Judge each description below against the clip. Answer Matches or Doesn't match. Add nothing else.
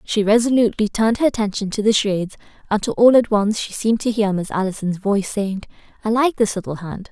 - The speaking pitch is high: Matches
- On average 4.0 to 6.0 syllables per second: Doesn't match